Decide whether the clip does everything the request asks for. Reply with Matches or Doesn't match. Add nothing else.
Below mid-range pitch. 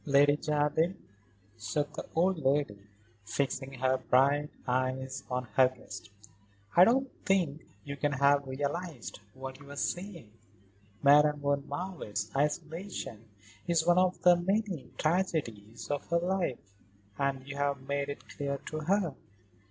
Doesn't match